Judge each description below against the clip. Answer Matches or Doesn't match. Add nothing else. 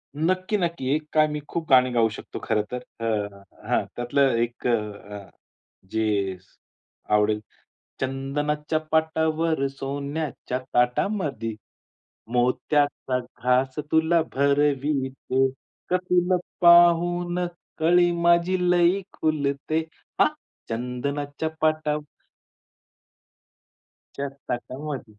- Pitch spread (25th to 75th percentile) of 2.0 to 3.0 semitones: Doesn't match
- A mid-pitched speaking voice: Matches